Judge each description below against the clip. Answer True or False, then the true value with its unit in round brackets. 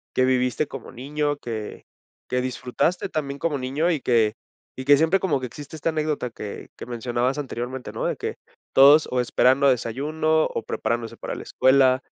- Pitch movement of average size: True (3.1 semitones)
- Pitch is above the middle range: False (130 Hz)